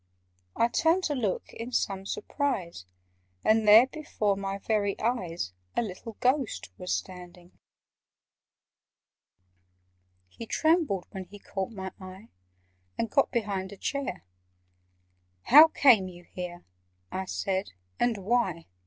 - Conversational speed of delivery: No, slow, 120 wpm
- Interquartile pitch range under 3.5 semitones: No, average, 4.5 semitones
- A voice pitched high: Yes, high, 200 Hz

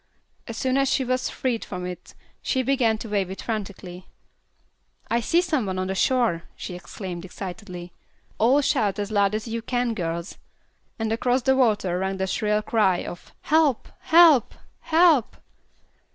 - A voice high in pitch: Yes, high, 220 Hz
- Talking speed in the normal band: Yes, average, 160 wpm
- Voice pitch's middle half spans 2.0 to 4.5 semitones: No, average, 5.2 semitones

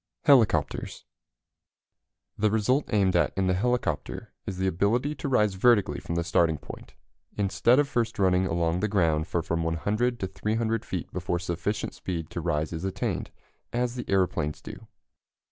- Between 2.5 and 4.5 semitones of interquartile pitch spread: No, average, 5.0 semitones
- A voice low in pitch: Yes, very low, 95 Hz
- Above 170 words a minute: No, average, 160 wpm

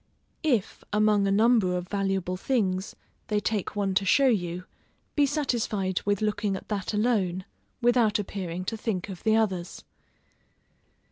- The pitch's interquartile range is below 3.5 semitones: Yes, average, 2.8 semitones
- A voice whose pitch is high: Yes, high, 205 Hz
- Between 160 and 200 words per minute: No, average, 145 wpm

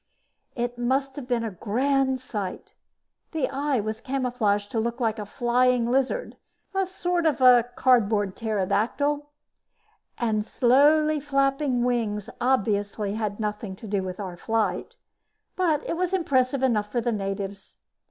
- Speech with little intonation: No, average, 4.4 semitones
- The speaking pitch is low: No, high, 240 Hz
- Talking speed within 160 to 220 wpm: No, average, 145 wpm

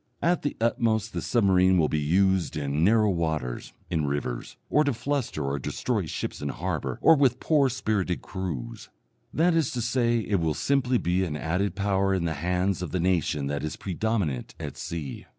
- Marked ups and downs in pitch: Yes, wide, 6.5 semitones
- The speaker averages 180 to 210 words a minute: Yes, average, 185 wpm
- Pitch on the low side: Yes, very low, 95 Hz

